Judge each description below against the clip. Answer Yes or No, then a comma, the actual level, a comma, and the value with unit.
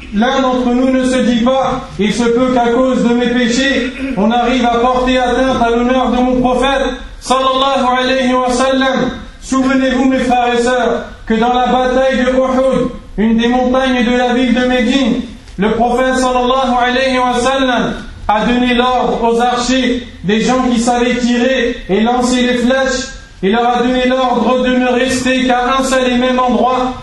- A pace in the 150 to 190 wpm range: Yes, average, 170 wpm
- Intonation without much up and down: Yes, narrow, 1.1 semitones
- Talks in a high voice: Yes, very high, 250 Hz